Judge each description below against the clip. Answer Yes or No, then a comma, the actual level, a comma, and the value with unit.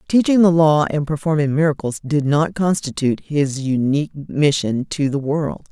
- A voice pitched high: No, medium, 150 Hz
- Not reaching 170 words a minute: Yes, average, 160 wpm